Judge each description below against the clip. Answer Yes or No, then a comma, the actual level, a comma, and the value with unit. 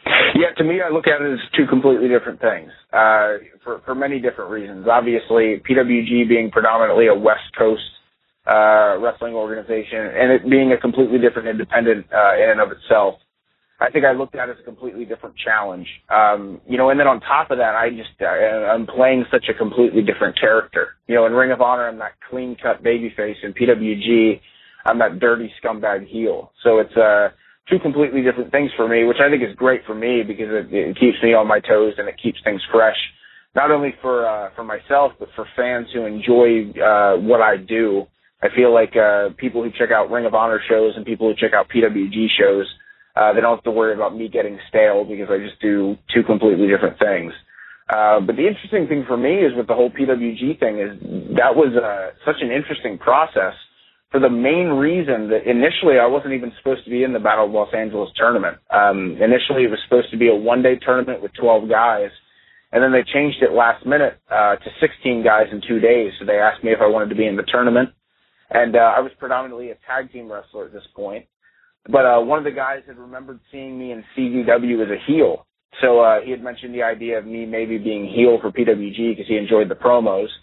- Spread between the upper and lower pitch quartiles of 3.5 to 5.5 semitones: No, average, 2.7 semitones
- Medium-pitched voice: No, low, 120 Hz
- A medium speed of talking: No, fast, 225 wpm